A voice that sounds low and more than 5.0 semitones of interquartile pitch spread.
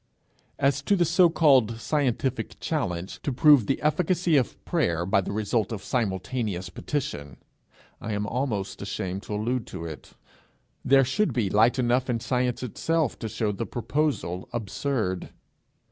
Yes: low, 120 Hz; wide, 5.6 semitones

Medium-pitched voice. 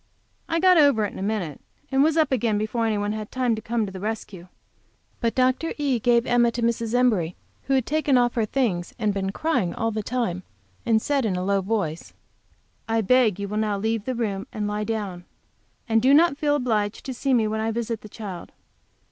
No: high, 225 Hz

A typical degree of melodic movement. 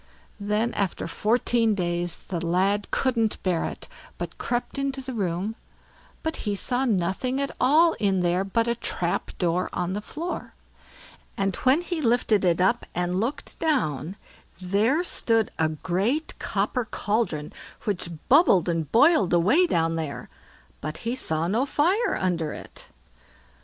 No: wide, 6.3 semitones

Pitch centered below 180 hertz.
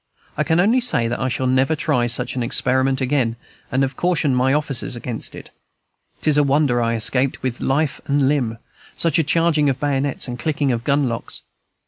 Yes: low, 135 Hz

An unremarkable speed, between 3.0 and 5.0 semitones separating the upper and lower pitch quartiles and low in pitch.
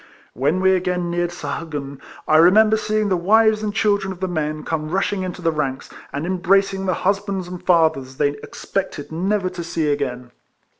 No: average, 180 wpm; average, 4.0 semitones; medium, 175 Hz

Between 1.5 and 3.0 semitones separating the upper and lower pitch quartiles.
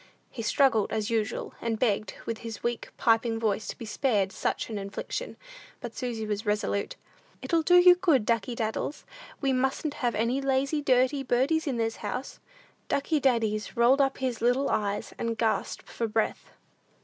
No: average, 3.5 semitones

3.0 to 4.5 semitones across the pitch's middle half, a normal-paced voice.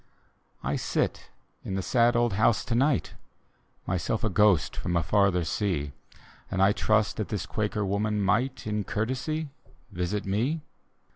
Yes: average, 3.5 semitones; average, 155 wpm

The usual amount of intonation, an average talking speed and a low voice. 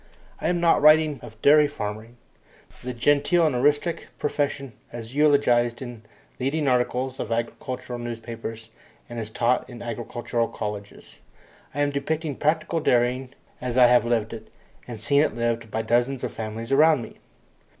Yes: average, 3.7 semitones; average, 155 wpm; low, 125 Hz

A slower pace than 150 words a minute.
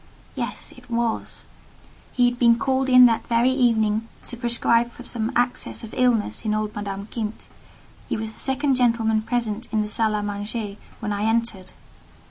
No: average, 175 wpm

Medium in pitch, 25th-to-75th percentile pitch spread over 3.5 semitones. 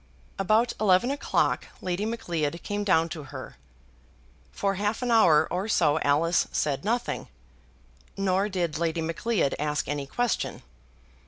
Yes: medium, 180 Hz; average, 5.2 semitones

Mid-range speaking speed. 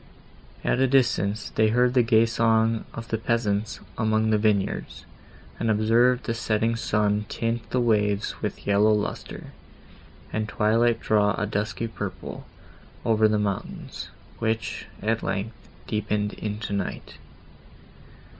No: slow, 130 wpm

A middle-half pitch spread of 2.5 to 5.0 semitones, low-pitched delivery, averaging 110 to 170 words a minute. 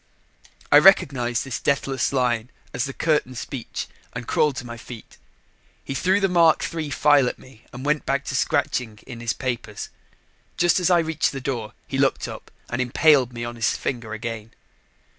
No: average, 3.8 semitones; low, 130 Hz; average, 180 wpm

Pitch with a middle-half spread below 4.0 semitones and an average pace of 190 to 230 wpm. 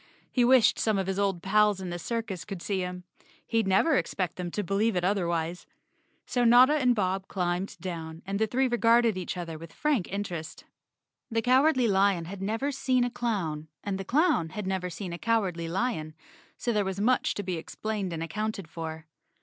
No: average, 4.6 semitones; average, 195 wpm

